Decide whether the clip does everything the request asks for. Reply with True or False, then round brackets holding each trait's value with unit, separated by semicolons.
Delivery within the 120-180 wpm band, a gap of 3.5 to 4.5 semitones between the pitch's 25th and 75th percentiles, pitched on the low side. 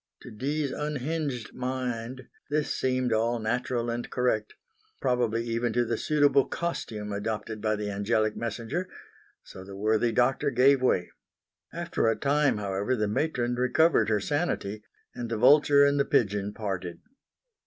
True (145 wpm; 4.0 semitones; 120 Hz)